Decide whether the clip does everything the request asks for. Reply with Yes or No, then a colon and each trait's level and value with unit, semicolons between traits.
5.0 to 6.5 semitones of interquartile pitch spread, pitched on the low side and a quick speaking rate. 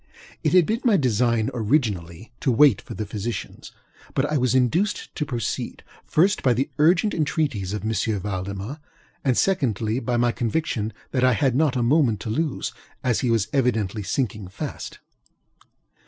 No: average, 5.3 semitones; low, 120 Hz; average, 165 wpm